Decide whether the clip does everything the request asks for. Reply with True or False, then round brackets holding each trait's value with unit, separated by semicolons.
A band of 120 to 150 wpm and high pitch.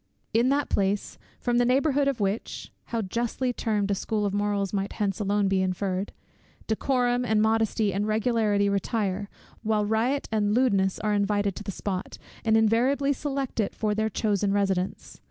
False (170 wpm; 210 Hz)